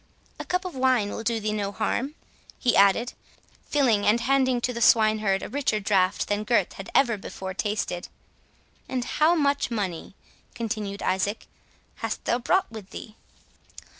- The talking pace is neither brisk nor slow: Yes, average, 160 wpm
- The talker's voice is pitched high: Yes, high, 220 Hz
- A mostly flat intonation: No, average, 3.9 semitones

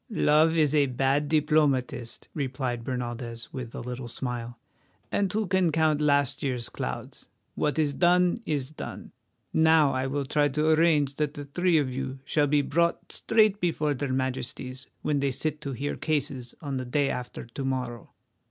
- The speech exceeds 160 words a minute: Yes, average, 170 wpm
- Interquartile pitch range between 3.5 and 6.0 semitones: No, average, 3.1 semitones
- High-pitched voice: No, medium, 140 Hz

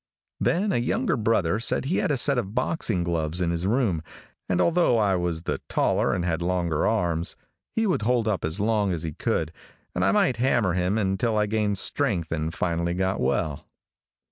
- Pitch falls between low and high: No, very low, 95 Hz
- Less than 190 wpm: No, average, 195 wpm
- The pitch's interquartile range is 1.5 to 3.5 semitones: No, average, 5.2 semitones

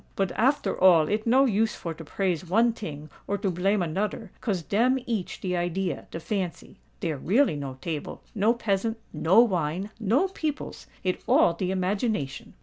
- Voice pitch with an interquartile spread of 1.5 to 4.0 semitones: No, average, 4.5 semitones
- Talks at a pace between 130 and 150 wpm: Yes, average, 145 wpm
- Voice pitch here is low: No, high, 195 Hz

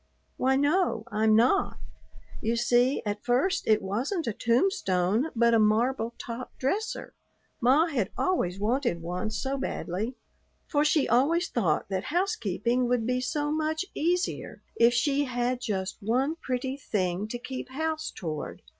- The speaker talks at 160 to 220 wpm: No, average, 145 wpm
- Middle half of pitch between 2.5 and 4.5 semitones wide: No, average, 4.9 semitones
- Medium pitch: No, high, 245 Hz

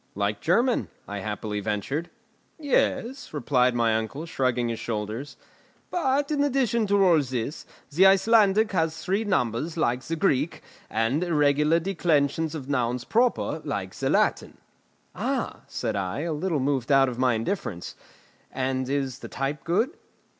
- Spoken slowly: No, average, 145 wpm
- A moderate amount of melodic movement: No, wide, 7.5 semitones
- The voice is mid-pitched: Yes, medium, 145 Hz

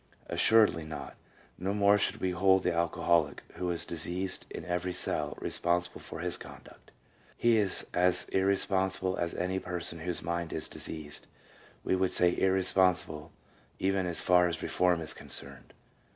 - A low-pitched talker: Yes, very low, 90 Hz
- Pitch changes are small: Yes, narrow, 1.8 semitones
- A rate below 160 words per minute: Yes, average, 150 wpm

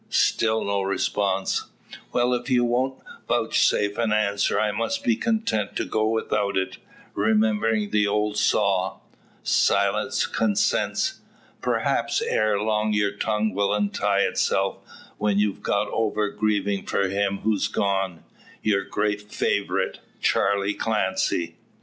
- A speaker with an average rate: No, slow, 125 wpm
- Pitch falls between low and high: No, low, 105 Hz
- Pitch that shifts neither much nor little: No, narrow, 1.5 semitones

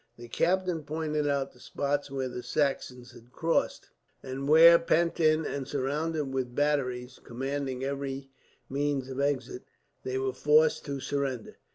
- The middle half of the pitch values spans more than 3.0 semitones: No, narrow, 2.5 semitones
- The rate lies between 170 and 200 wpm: No, average, 150 wpm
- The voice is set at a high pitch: No, medium, 140 Hz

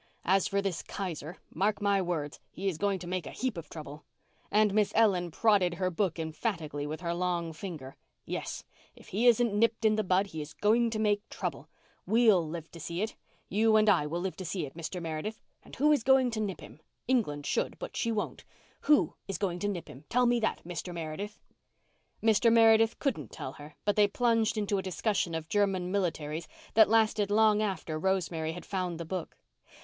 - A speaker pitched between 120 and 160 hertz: No, high, 195 Hz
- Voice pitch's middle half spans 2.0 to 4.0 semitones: No, average, 4.4 semitones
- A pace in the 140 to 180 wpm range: No, average, 200 wpm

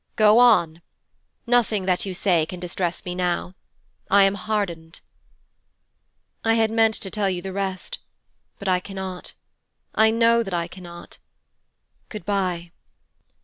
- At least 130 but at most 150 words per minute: Yes, average, 140 wpm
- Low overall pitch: No, high, 190 Hz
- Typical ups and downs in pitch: Yes, average, 3.3 semitones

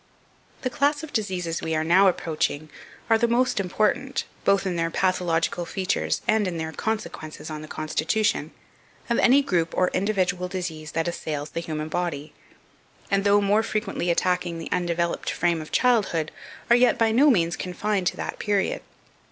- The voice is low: No, medium, 180 Hz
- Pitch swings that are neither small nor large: Yes, average, 4.5 semitones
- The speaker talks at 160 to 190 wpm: Yes, average, 170 wpm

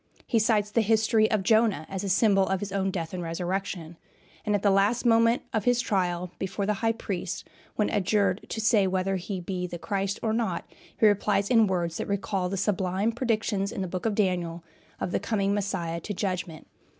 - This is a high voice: Yes, high, 195 Hz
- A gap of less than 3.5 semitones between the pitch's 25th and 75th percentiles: Yes, average, 2.9 semitones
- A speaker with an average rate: No, fast, 210 wpm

